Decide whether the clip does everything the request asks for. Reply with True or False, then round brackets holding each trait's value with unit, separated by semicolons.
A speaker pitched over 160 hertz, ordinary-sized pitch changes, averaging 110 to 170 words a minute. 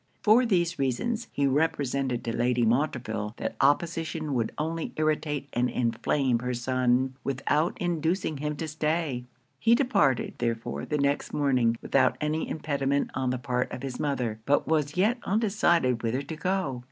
False (140 Hz; 4.3 semitones; 155 wpm)